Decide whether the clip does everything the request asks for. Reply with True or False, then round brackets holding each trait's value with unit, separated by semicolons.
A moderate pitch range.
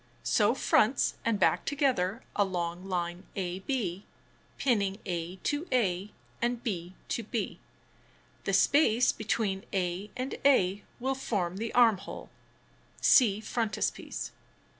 True (4.7 semitones)